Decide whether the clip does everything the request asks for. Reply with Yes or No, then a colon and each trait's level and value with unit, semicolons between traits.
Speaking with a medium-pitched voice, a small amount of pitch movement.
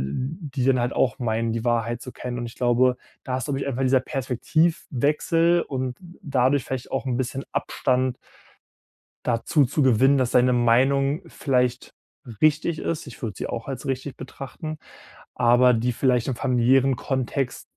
No: low, 130 Hz; narrow, 2.1 semitones